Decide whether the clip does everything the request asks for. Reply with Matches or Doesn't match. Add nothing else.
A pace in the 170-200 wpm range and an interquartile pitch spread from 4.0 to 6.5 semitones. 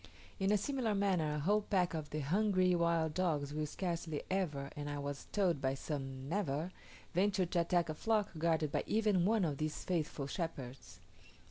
Matches